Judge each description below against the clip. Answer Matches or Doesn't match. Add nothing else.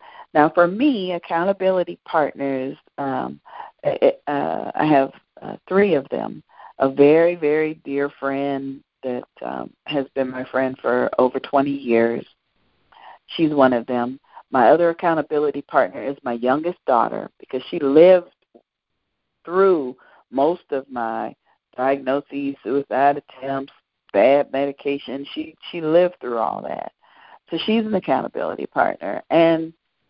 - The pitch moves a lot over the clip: Doesn't match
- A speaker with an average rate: Doesn't match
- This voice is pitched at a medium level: Matches